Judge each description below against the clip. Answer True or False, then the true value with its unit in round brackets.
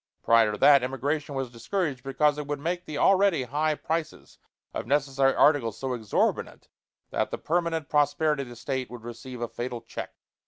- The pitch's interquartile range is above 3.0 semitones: True (3.5 semitones)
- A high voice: False (140 Hz)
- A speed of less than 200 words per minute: True (180 wpm)